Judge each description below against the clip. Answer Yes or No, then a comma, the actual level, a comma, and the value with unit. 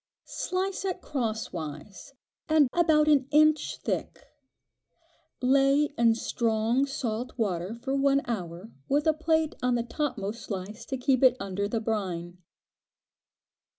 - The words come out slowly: Yes, slow, 125 wpm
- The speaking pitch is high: Yes, high, 245 Hz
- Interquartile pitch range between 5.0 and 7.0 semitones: Yes, wide, 5.4 semitones